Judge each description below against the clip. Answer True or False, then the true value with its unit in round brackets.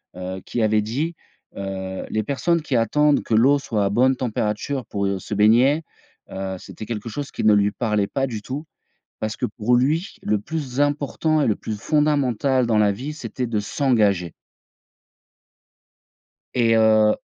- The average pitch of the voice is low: True (115 Hz)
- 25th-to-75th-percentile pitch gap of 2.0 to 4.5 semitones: False (5.0 semitones)